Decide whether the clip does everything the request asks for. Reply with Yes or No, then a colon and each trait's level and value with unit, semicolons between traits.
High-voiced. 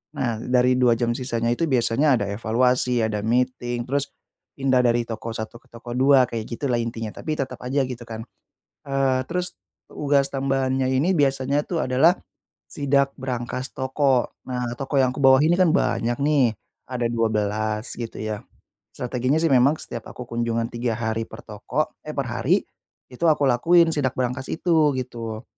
No: low, 125 Hz